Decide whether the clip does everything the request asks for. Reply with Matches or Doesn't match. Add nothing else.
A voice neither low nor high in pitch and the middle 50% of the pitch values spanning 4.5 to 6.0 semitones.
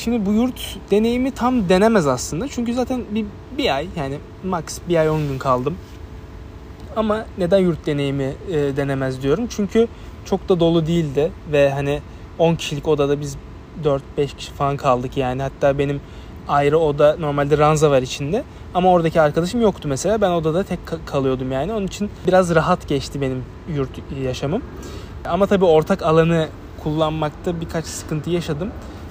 Matches